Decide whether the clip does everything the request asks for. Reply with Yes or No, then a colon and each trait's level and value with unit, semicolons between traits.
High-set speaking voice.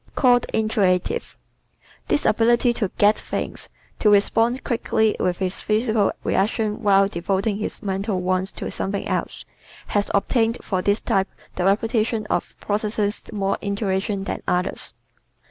Yes: high, 205 Hz